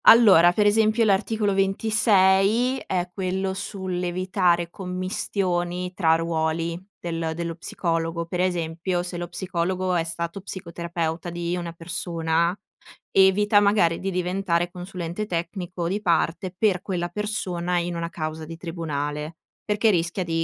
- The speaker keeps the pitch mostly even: Yes, narrow, 2.3 semitones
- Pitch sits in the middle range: Yes, medium, 175 Hz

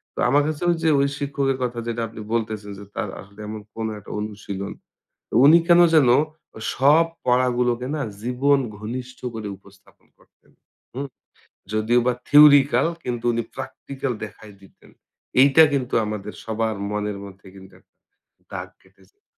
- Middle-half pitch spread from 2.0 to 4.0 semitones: No, average, 4.5 semitones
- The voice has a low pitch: Yes, low, 120 Hz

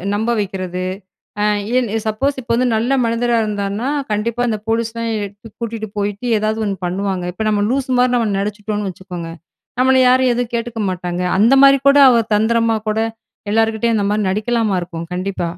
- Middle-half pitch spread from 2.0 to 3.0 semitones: Yes, average, 2.7 semitones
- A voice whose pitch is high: Yes, high, 220 Hz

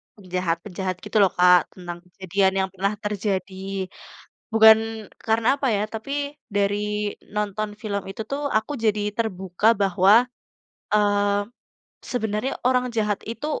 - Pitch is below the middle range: No, high, 210 Hz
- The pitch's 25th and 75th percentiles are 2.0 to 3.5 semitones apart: Yes, narrow, 2.4 semitones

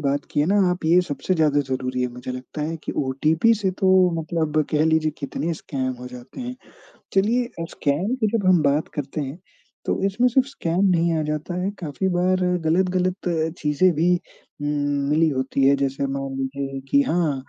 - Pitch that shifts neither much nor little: Yes, average, 4.7 semitones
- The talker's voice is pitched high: No, medium, 155 Hz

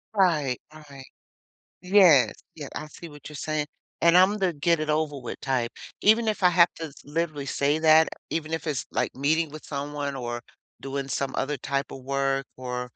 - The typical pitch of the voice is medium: Yes, medium, 150 Hz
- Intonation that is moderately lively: Yes, average, 3.0 semitones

